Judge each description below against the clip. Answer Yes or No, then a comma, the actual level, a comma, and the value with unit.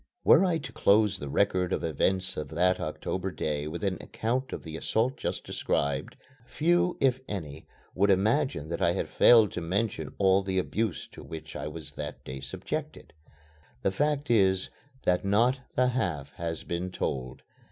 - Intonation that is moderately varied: No, wide, 5.8 semitones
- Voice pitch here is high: No, very low, 95 Hz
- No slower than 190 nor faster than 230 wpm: No, average, 175 wpm